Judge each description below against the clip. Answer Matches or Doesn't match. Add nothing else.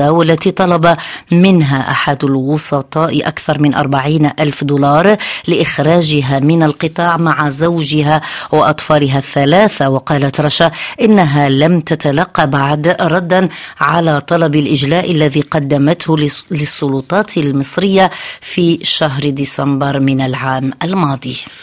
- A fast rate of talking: Doesn't match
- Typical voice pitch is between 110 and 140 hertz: Doesn't match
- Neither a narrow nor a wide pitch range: Matches